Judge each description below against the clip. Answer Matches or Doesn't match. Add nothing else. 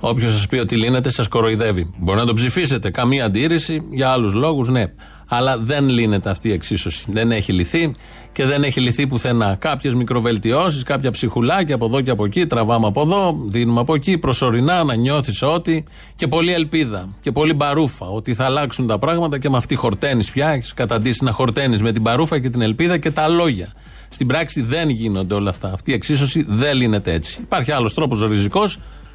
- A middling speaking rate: Doesn't match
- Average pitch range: Matches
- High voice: Doesn't match